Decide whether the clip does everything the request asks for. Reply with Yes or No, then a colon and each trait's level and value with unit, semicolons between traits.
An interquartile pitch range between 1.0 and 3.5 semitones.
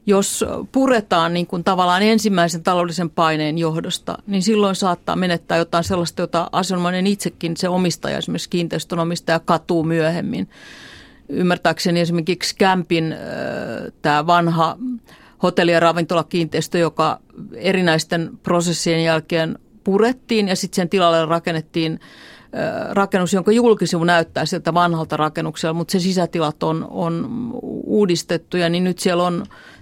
Yes: narrow, 2.4 semitones